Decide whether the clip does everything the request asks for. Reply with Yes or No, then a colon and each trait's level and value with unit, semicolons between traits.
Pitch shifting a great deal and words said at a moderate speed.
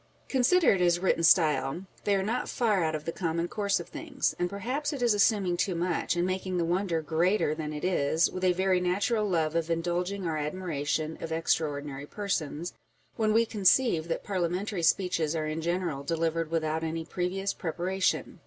No: average, 3.2 semitones; average, 185 wpm